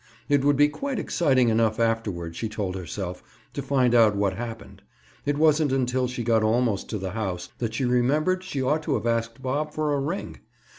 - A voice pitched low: Yes, low, 120 Hz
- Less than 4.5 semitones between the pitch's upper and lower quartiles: No, average, 4.8 semitones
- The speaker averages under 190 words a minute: No, average, 200 wpm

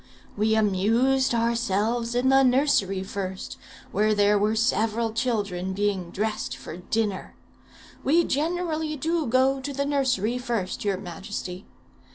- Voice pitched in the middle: No, high, 225 Hz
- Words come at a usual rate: No, slow, 130 wpm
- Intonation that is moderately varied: Yes, average, 4.5 semitones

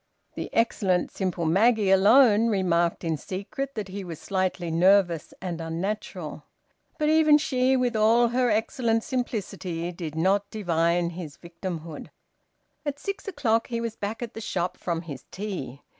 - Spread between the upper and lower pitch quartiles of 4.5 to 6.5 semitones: Yes, average, 5.2 semitones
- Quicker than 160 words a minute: No, average, 150 wpm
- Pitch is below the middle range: No, high, 195 Hz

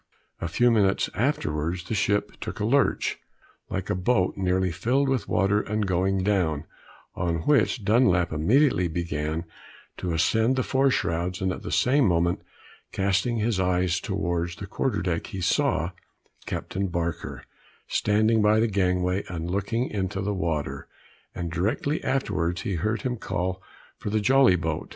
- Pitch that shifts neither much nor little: Yes, average, 3.9 semitones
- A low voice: Yes, very low, 95 Hz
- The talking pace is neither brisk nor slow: Yes, average, 155 wpm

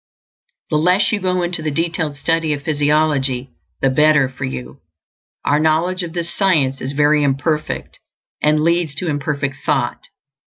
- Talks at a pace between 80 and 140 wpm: No, average, 155 wpm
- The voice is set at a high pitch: No, medium, 150 Hz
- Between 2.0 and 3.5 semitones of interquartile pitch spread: Yes, average, 3.0 semitones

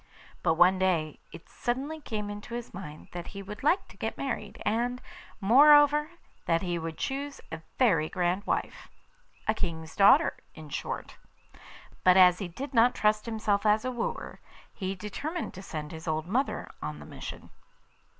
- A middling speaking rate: Yes, average, 170 wpm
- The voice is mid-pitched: No, high, 205 Hz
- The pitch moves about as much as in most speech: No, wide, 5.9 semitones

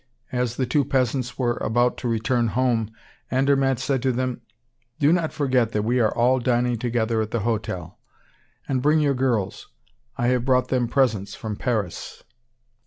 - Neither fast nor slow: Yes, average, 170 wpm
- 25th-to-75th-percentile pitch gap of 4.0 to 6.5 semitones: No, narrow, 2.4 semitones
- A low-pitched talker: Yes, low, 125 Hz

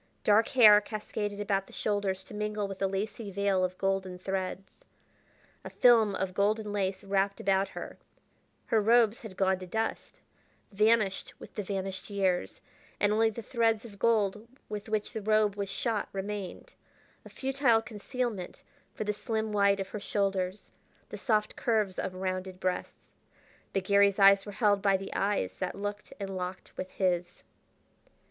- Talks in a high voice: Yes, high, 200 Hz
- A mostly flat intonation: Yes, narrow, 1.9 semitones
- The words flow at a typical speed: Yes, average, 165 wpm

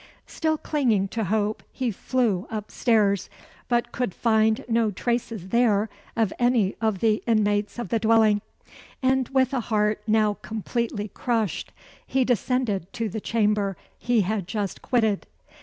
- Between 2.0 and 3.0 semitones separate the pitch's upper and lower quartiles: Yes, narrow, 2.6 semitones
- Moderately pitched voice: No, high, 220 Hz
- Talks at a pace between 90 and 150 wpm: Yes, average, 145 wpm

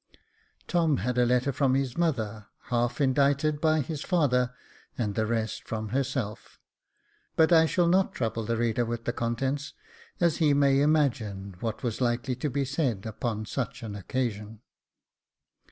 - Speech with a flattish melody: No, average, 4.1 semitones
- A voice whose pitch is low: Yes, low, 125 Hz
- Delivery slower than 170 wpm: Yes, average, 155 wpm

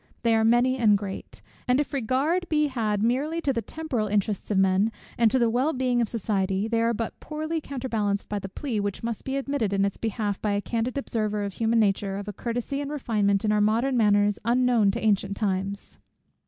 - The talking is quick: Yes, fast, 215 wpm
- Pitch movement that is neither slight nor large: Yes, average, 3.9 semitones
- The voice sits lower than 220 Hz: No, high, 225 Hz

